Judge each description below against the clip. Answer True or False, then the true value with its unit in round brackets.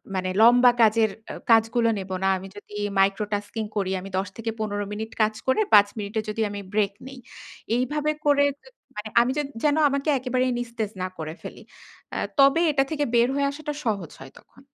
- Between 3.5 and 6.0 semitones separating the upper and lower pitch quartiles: True (4.1 semitones)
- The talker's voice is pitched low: False (225 Hz)